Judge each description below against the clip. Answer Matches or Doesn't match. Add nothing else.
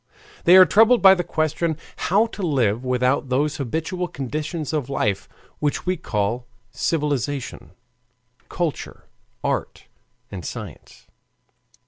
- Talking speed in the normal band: Doesn't match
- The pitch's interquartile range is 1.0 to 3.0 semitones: Doesn't match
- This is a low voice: Doesn't match